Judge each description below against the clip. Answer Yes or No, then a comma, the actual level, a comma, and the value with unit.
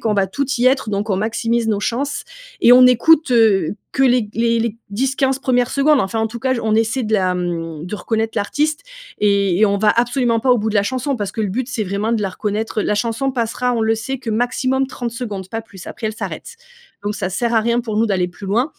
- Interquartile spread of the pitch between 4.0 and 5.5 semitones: No, average, 3.3 semitones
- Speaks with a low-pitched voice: No, high, 225 Hz